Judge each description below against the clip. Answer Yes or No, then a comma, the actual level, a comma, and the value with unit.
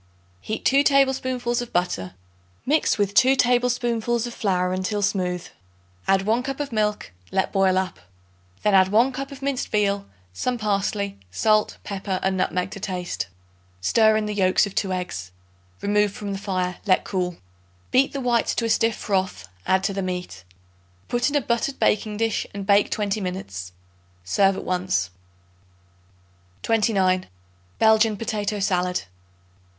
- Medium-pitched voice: No, high, 205 Hz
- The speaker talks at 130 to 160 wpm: Yes, average, 155 wpm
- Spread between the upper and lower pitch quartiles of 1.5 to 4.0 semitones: Yes, average, 3.6 semitones